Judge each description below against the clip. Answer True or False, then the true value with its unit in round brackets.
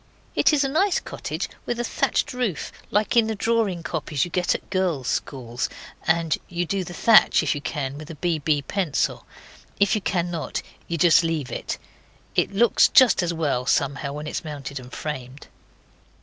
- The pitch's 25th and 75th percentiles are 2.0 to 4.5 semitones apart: False (5.5 semitones)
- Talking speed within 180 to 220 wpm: True (185 wpm)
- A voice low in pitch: False (170 Hz)